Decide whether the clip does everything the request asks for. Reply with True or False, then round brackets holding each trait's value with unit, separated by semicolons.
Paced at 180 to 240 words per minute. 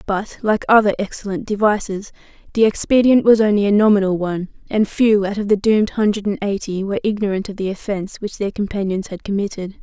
True (190 wpm)